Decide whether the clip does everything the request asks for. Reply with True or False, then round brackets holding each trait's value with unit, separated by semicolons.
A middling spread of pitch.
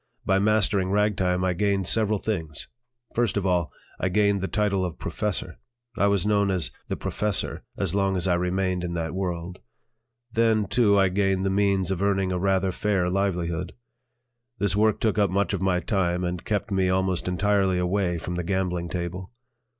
False (2.1 semitones)